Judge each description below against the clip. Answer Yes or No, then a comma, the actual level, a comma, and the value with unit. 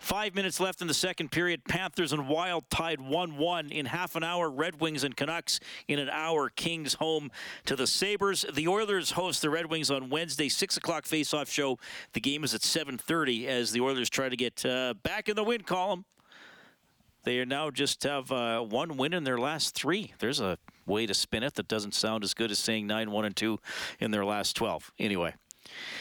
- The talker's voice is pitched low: No, medium, 155 Hz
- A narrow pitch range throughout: No, average, 5.3 semitones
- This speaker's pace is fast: Yes, fast, 210 wpm